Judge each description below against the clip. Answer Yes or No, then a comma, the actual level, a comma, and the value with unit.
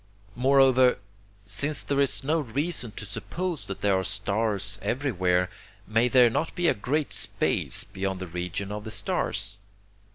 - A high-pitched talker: No, low, 110 Hz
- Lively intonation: Yes, wide, 5.8 semitones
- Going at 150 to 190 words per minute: Yes, average, 155 wpm